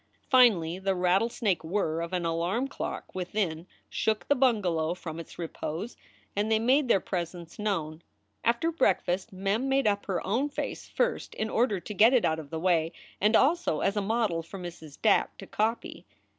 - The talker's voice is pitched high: Yes, high, 195 Hz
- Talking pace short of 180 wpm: No, average, 185 wpm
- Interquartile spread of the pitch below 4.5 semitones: No, average, 5.2 semitones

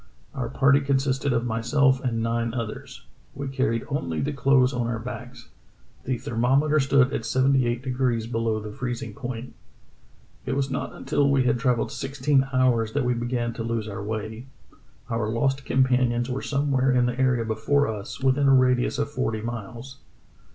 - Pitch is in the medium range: No, low, 125 Hz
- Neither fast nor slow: Yes, average, 170 wpm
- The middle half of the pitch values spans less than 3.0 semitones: Yes, narrow, 2.6 semitones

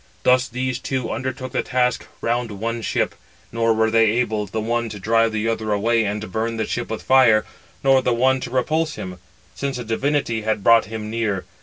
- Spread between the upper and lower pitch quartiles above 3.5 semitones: No, narrow, 2.5 semitones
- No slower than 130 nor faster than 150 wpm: No, average, 200 wpm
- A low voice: Yes, low, 115 Hz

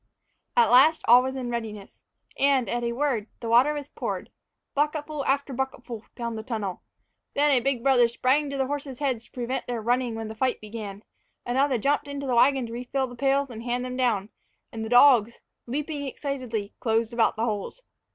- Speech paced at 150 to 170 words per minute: No, average, 195 wpm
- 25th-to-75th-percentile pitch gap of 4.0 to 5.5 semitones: No, average, 3.1 semitones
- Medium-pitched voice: No, very high, 250 Hz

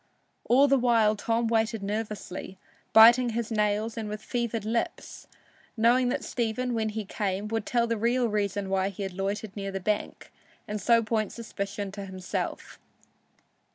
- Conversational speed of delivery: Yes, average, 160 wpm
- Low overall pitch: No, high, 220 Hz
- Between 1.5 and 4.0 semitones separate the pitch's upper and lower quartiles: Yes, narrow, 2.5 semitones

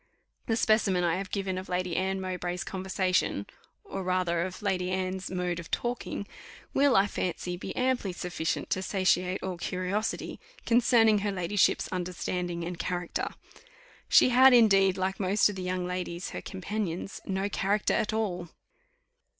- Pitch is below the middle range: No, medium, 185 Hz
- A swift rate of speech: No, average, 150 wpm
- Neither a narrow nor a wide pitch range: No, narrow, 2.1 semitones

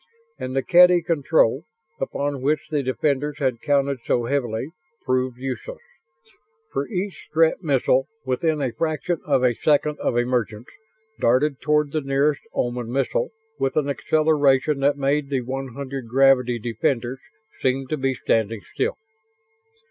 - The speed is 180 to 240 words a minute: No, average, 140 wpm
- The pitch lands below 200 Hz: Yes, low, 135 Hz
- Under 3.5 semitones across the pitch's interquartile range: Yes, average, 2.9 semitones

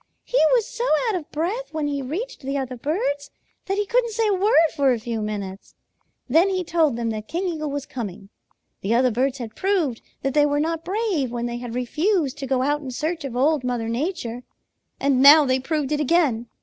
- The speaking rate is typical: No, fast, 215 wpm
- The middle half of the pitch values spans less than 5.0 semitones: No, wide, 5.4 semitones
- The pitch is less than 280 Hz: No, very high, 285 Hz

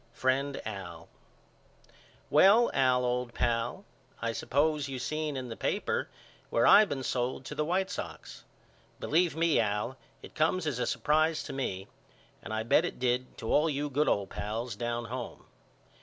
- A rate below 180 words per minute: Yes, average, 165 wpm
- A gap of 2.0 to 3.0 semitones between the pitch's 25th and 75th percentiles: No, average, 4.6 semitones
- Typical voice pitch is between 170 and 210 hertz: No, low, 130 Hz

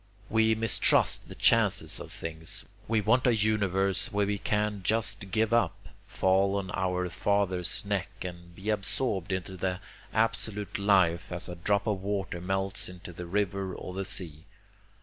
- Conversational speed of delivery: Yes, average, 160 wpm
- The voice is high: No, very low, 95 Hz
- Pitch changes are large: No, narrow, 2.4 semitones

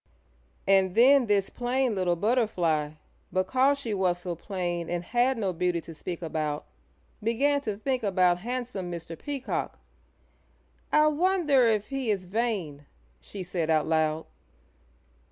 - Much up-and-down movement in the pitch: Yes, wide, 6.1 semitones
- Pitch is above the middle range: Yes, high, 195 Hz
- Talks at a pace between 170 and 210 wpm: No, slow, 135 wpm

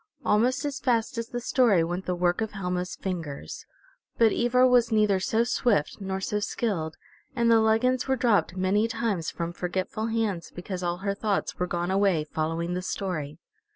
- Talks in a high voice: Yes, high, 200 Hz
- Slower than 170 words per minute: No, average, 180 wpm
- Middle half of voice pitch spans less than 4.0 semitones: No, average, 4.4 semitones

